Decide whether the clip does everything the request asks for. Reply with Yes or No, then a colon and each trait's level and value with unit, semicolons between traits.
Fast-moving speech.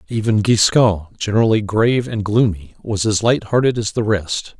No: average, 170 wpm